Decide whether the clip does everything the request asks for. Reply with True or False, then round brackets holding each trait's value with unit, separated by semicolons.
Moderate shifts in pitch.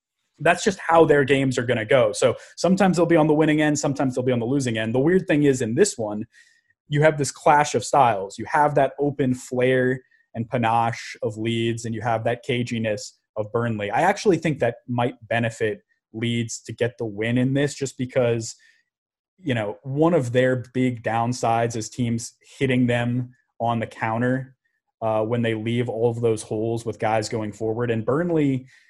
True (3.6 semitones)